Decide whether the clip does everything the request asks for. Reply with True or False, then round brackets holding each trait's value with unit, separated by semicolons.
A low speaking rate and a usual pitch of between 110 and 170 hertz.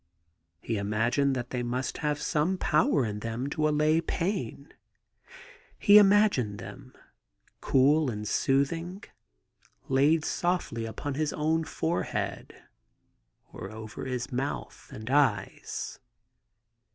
True (110 wpm; 140 Hz)